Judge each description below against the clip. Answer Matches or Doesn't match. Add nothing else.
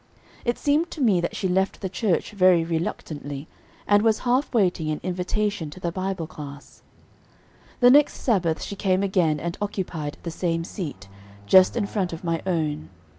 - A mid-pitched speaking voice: Matches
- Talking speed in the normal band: Matches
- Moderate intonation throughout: Matches